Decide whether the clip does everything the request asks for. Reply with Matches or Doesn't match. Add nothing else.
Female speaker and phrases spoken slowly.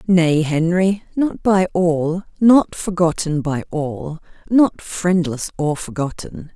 Matches